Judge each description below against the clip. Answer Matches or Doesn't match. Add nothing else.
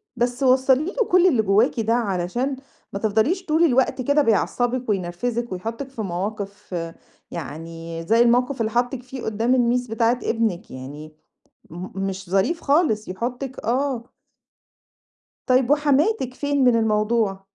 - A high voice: Matches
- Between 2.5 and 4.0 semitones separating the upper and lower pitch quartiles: Doesn't match